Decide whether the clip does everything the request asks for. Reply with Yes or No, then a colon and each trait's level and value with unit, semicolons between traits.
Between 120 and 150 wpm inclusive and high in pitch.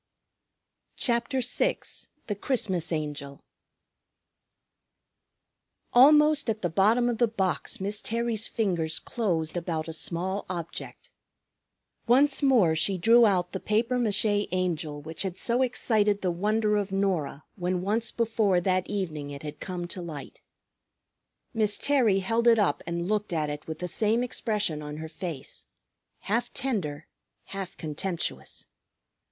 Yes: slow, 135 wpm; high, 195 Hz